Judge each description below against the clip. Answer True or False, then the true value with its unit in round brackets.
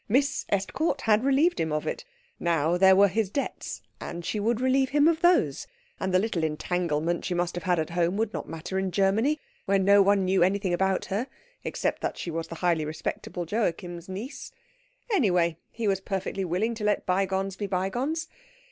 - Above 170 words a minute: True (190 wpm)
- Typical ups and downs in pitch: True (4.2 semitones)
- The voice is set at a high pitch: True (195 Hz)